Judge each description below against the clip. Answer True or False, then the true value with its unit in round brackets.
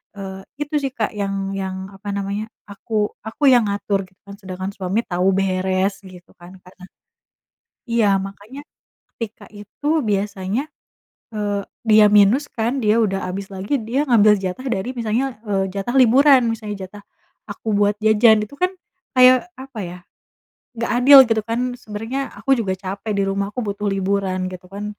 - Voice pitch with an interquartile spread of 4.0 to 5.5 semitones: False (2.8 semitones)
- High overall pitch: True (205 Hz)